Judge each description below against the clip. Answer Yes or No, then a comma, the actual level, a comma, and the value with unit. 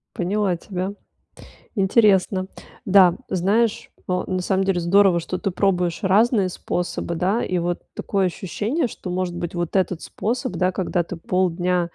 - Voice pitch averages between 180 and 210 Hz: Yes, medium, 185 Hz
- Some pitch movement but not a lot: No, narrow, 2.1 semitones